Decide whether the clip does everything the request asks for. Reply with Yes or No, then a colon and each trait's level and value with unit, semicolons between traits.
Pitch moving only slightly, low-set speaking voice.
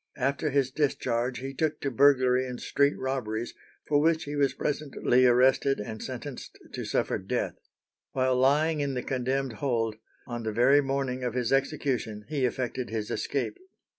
Yes: narrow, 2.3 semitones; low, 130 Hz